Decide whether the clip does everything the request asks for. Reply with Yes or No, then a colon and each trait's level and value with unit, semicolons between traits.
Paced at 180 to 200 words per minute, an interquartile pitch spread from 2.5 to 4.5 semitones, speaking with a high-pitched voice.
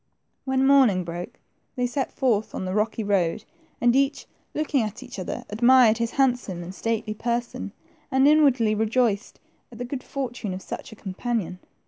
No: average, 165 wpm; average, 3.9 semitones; high, 235 Hz